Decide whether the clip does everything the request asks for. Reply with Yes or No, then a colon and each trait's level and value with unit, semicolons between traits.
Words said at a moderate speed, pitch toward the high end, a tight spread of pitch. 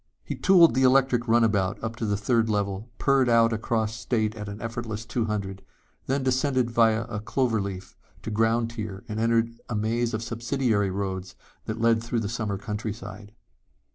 No: average, 170 wpm; low, 115 Hz; narrow, 2.2 semitones